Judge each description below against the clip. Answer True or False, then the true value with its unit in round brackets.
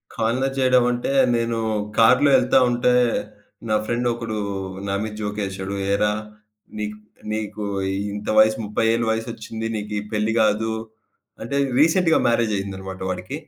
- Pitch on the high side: False (110 Hz)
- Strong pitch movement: False (2.4 semitones)